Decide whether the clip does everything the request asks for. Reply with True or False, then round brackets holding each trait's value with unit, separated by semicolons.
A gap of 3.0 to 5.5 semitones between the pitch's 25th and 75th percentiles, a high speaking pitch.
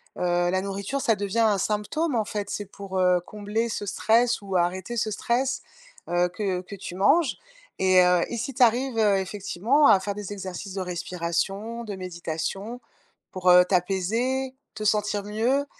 True (3.6 semitones; 200 Hz)